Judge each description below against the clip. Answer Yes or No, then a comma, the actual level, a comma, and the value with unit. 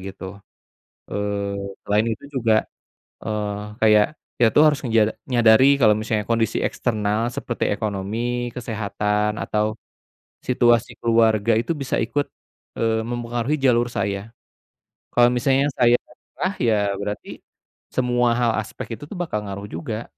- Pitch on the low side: Yes, low, 115 Hz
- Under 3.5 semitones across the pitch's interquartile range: Yes, narrow, 2.5 semitones